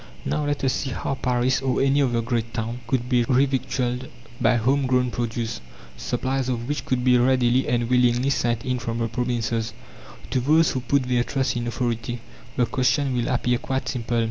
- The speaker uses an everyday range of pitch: No, narrow, 1.7 semitones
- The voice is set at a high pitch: No, low, 125 Hz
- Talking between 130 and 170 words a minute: No, average, 190 wpm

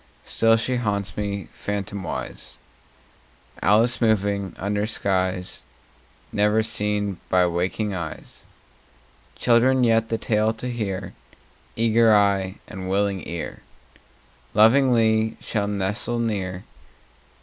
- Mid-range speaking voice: No, low, 105 Hz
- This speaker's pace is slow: Yes, slow, 100 wpm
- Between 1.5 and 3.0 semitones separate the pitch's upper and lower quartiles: Yes, narrow, 2.5 semitones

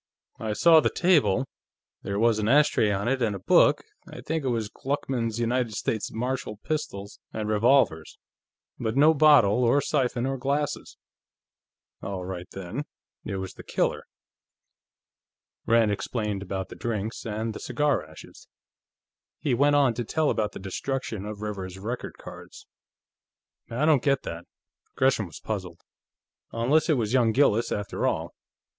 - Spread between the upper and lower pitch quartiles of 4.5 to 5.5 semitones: Yes, average, 4.8 semitones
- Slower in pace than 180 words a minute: Yes, average, 150 wpm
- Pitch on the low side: Yes, low, 115 Hz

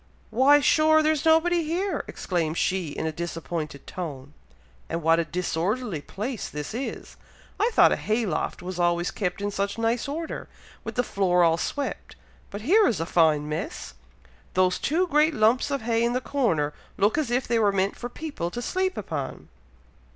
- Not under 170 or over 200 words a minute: Yes, average, 180 wpm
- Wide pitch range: Yes, wide, 8.5 semitones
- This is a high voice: Yes, high, 210 Hz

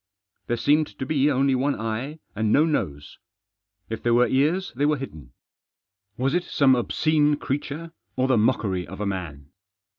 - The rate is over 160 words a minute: Yes, average, 170 wpm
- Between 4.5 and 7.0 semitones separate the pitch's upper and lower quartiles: Yes, average, 5.1 semitones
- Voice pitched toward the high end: No, low, 130 Hz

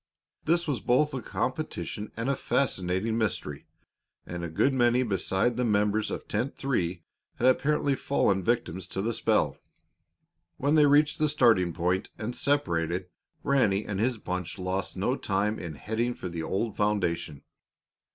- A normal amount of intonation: No, wide, 5.9 semitones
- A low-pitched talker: Yes, low, 110 Hz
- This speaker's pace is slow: No, average, 155 wpm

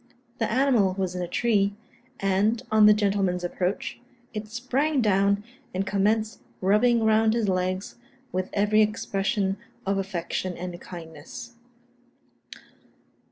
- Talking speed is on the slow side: Yes, slow, 120 wpm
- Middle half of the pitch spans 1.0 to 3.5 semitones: Yes, average, 2.7 semitones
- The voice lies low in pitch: No, high, 200 Hz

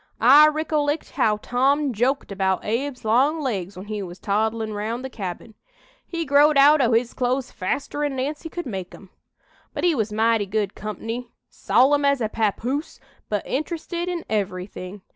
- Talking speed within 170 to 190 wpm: No, average, 160 wpm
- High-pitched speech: Yes, high, 245 Hz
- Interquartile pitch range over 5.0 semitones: Yes, wide, 5.4 semitones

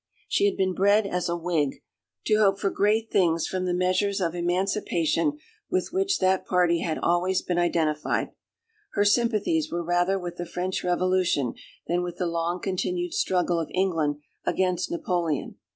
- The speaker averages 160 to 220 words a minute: Yes, average, 165 wpm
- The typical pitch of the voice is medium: Yes, medium, 180 Hz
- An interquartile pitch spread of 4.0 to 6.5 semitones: No, average, 2.7 semitones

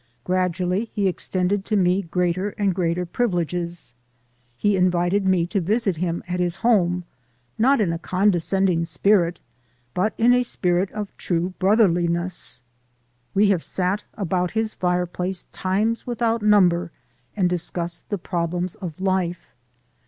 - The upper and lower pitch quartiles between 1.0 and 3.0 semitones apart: Yes, narrow, 2.6 semitones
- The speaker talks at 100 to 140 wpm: Yes, slow, 135 wpm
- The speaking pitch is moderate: Yes, medium, 180 Hz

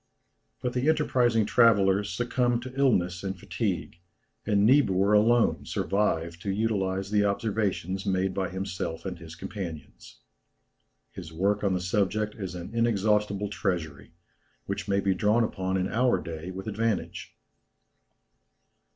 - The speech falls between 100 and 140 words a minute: Yes, slow, 135 wpm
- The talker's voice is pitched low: Yes, low, 100 Hz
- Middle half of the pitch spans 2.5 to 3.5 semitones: Yes, average, 2.9 semitones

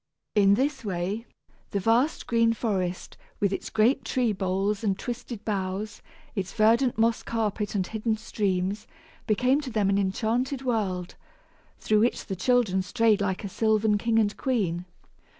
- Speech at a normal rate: Yes, average, 150 wpm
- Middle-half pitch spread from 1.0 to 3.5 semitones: Yes, average, 2.9 semitones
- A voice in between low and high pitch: No, high, 215 Hz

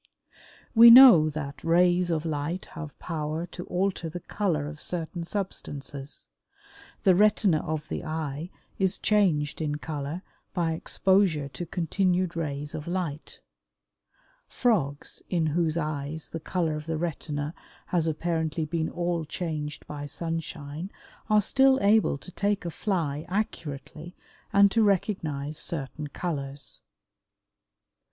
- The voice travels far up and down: No, average, 3.4 semitones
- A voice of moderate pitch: Yes, medium, 165 Hz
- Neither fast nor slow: No, slow, 130 wpm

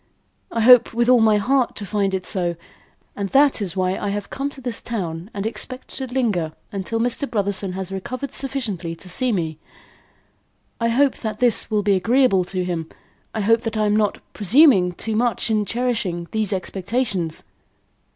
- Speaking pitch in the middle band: No, high, 210 Hz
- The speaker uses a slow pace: No, average, 180 wpm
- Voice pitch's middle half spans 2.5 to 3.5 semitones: No, average, 4.4 semitones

